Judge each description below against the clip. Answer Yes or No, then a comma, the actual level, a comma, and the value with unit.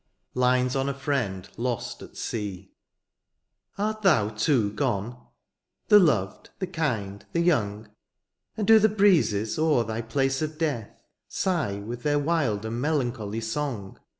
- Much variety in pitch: Yes, wide, 6.6 semitones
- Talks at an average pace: Yes, average, 145 wpm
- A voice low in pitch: Yes, low, 125 Hz